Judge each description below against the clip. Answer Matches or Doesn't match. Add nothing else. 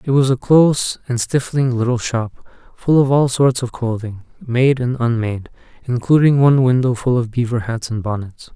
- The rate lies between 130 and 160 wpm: Doesn't match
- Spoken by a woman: Doesn't match